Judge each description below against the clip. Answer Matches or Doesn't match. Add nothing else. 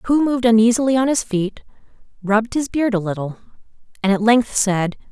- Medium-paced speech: Matches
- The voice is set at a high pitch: Matches